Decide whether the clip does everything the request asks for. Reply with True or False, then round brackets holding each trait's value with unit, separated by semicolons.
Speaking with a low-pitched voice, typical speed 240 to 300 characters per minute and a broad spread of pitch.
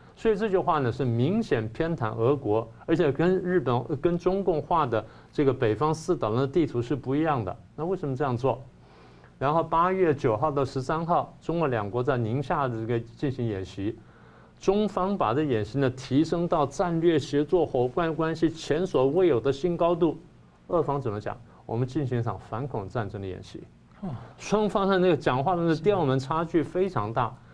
False (145 Hz; 275 characters per minute; 6.1 semitones)